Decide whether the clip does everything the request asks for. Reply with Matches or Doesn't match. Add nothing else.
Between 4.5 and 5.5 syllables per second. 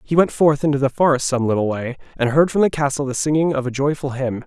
Doesn't match